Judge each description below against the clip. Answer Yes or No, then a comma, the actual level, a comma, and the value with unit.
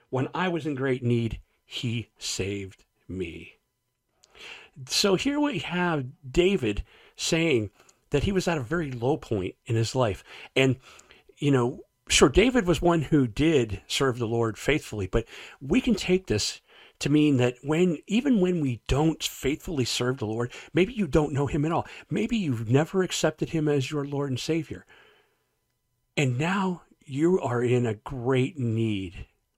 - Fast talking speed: No, average, 165 wpm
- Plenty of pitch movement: Yes, wide, 5.8 semitones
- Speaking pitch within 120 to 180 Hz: Yes, medium, 140 Hz